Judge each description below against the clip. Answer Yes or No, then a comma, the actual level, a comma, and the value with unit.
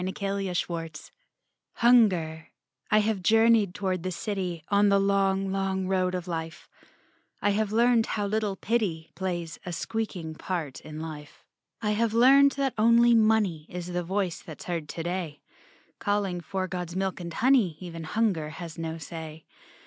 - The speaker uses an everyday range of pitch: Yes, average, 4.0 semitones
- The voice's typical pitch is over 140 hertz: Yes, high, 190 Hz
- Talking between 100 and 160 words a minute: Yes, average, 155 wpm